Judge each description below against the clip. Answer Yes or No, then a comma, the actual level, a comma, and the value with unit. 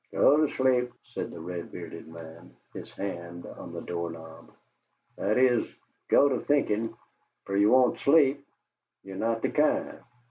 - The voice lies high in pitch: No, low, 105 Hz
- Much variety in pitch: Yes, wide, 7.2 semitones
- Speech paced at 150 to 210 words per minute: Yes, average, 155 wpm